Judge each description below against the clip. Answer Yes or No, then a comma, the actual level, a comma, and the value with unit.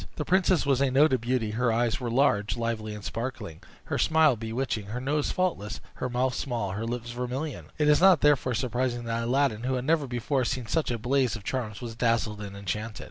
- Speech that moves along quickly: Yes, fast, 210 wpm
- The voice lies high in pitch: No, low, 125 Hz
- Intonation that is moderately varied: Yes, average, 3.3 semitones